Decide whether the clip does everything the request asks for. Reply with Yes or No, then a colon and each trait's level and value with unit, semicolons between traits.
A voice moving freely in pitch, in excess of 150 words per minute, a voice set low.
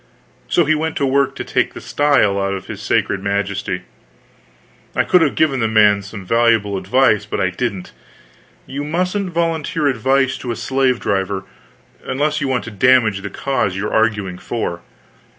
Yes: wide, 5.9 semitones; average, 175 wpm; low, 115 Hz